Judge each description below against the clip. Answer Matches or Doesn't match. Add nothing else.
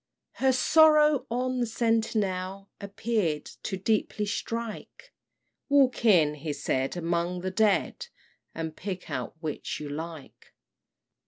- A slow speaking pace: Matches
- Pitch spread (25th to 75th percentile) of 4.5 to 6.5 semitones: Matches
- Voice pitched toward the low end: Doesn't match